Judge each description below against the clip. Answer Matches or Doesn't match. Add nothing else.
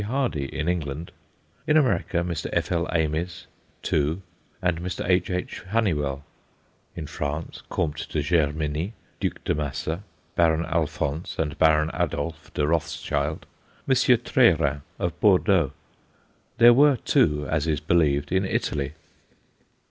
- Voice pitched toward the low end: Matches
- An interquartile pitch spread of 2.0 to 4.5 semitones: Matches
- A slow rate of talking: Matches